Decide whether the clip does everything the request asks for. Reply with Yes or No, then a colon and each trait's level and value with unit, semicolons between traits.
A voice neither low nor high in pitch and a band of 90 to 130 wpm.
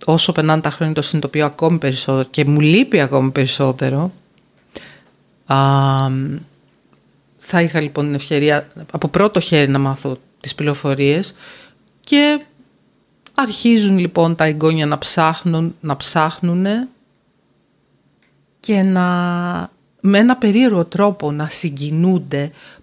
Yes: medium, 160 Hz; slow, 115 wpm